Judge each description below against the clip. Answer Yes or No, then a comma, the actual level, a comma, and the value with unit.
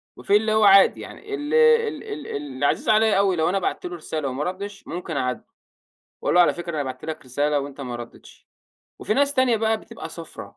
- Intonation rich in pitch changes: Yes, wide, 7.3 semitones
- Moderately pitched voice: Yes, medium, 180 Hz